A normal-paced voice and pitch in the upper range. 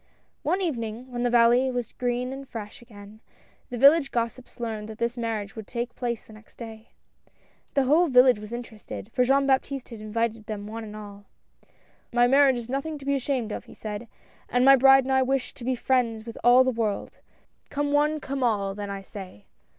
No: fast, 210 wpm; high, 240 Hz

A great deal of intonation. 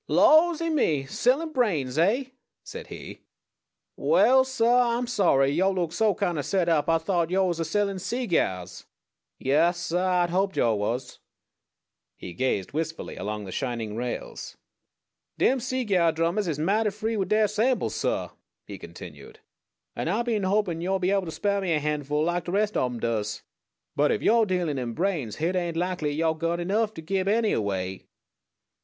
Yes: wide, 6.0 semitones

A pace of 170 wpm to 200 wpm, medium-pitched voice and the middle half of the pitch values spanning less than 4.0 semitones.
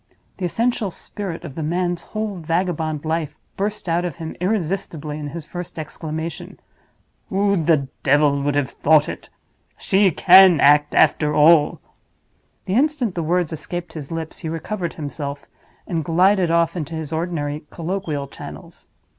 No: average, 150 wpm; medium, 165 Hz; average, 3.2 semitones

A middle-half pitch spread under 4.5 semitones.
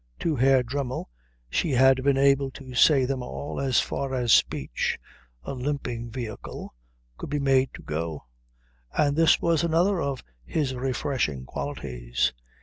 Yes: average, 2.7 semitones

